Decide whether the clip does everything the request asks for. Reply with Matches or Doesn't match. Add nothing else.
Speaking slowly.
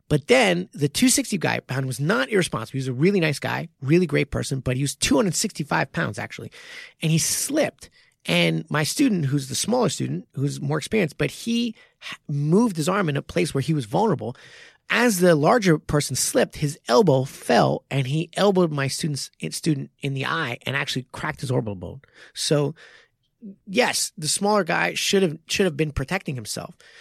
Doesn't match